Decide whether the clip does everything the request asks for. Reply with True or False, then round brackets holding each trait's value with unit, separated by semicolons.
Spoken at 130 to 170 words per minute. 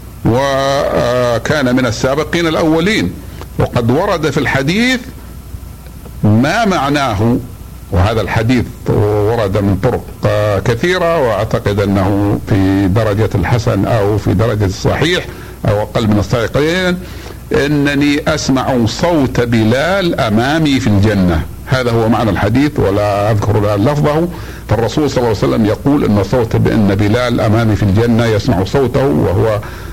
False (120 wpm)